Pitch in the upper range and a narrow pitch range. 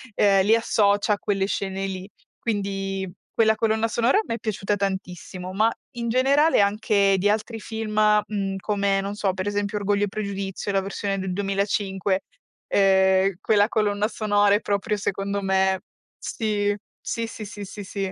Yes: high, 200 Hz; narrow, 1.6 semitones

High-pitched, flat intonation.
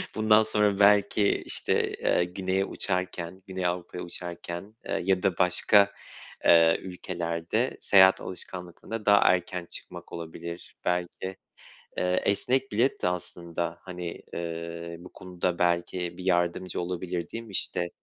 No: very low, 90 Hz; narrow, 2.1 semitones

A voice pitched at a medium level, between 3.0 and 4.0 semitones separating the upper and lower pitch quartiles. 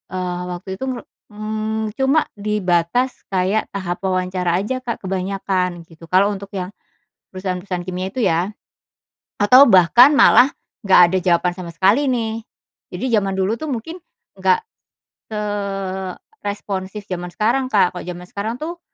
No: high, 195 Hz; average, 3.3 semitones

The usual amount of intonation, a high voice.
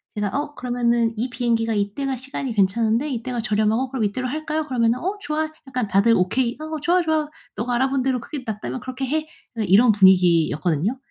Yes: average, 4.0 semitones; high, 240 Hz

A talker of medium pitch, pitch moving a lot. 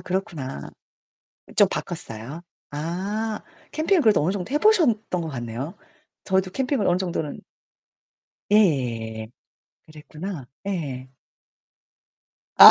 Yes: medium, 175 Hz; wide, 7.5 semitones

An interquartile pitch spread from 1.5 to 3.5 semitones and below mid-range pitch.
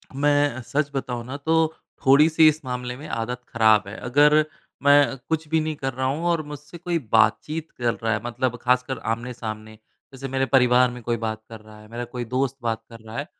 No: average, 3.9 semitones; low, 130 Hz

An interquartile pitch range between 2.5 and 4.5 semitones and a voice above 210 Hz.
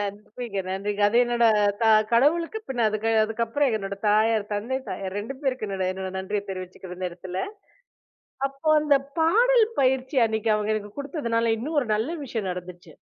No: average, 5.0 semitones; high, 220 Hz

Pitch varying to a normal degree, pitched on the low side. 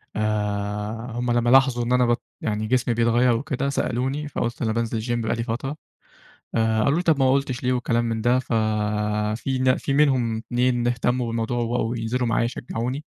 No: narrow, 1.9 semitones; low, 120 Hz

